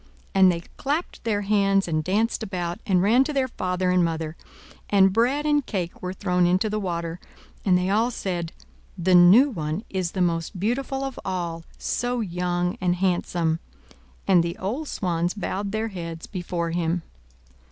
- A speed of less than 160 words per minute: No, average, 170 wpm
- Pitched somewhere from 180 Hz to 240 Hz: Yes, medium, 185 Hz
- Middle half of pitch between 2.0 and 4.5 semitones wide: Yes, average, 3.6 semitones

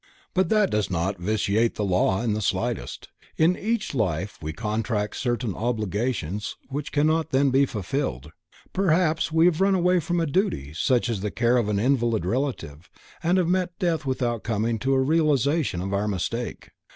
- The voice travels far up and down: Yes, wide, 7.3 semitones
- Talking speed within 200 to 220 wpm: No, average, 175 wpm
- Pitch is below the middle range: Yes, low, 120 Hz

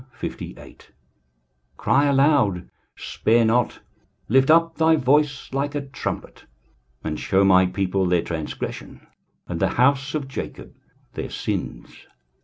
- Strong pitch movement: Yes, wide, 6.8 semitones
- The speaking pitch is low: Yes, low, 130 Hz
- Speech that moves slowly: Yes, slow, 120 wpm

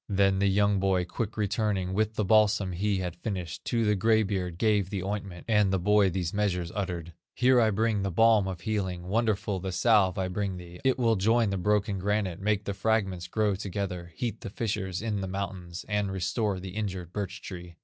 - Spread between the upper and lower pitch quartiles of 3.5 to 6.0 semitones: No, narrow, 2.5 semitones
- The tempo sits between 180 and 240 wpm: Yes, fast, 205 wpm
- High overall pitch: No, low, 100 Hz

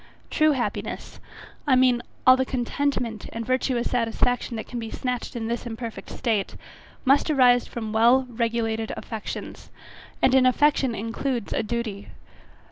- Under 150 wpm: Yes, average, 140 wpm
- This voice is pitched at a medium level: No, high, 240 Hz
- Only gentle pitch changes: Yes, narrow, 2.2 semitones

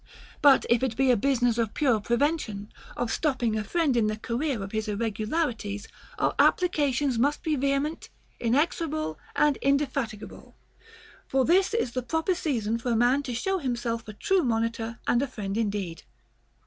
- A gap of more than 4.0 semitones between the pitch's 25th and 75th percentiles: Yes, average, 4.5 semitones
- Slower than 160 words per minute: No, average, 170 wpm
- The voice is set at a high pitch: Yes, high, 245 Hz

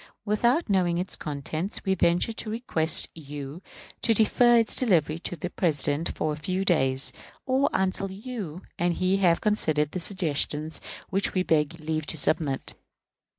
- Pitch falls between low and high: Yes, medium, 175 Hz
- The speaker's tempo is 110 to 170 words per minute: Yes, average, 155 wpm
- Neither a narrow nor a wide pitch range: Yes, average, 4.4 semitones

